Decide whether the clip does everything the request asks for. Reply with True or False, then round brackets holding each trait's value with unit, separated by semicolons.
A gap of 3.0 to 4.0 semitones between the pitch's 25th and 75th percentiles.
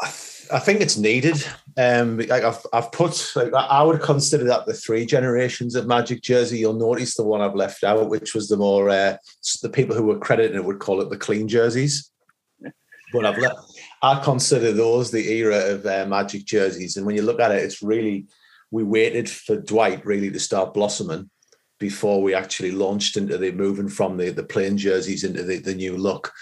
True (3.6 semitones)